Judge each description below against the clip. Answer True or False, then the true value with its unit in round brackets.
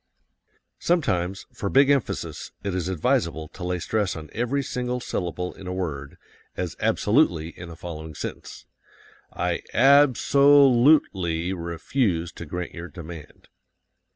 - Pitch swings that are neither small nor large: False (6.9 semitones)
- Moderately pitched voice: False (90 Hz)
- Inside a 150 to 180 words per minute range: False (140 wpm)